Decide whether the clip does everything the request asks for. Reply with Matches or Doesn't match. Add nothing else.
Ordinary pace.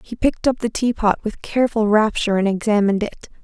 Matches